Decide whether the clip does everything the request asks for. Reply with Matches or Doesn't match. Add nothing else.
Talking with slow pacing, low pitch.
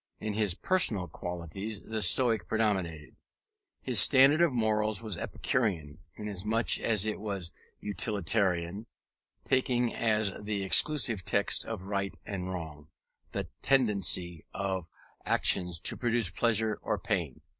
Matches